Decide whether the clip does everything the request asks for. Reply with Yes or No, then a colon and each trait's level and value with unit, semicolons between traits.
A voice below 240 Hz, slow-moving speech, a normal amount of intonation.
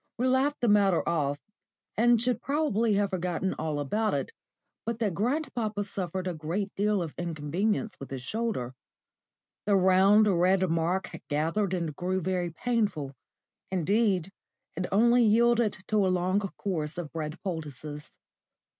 No: high, 190 Hz; average, 145 wpm; average, 4.4 semitones